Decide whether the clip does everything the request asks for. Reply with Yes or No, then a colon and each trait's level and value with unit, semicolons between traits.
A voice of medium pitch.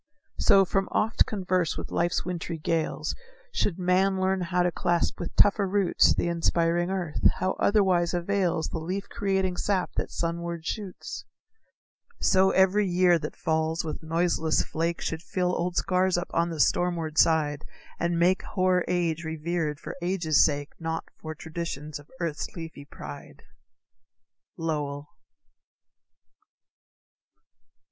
Yes: medium, 170 Hz